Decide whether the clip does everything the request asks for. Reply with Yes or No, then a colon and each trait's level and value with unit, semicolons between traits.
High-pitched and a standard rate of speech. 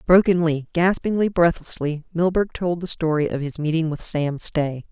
No: medium, 165 Hz; average, 160 wpm